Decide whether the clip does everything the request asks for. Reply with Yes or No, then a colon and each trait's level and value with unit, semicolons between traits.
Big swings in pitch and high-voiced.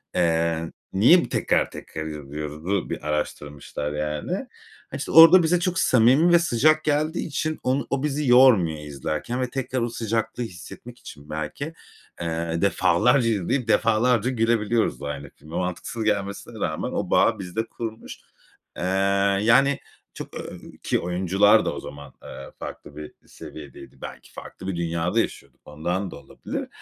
No: wide, 7.7 semitones; low, 100 Hz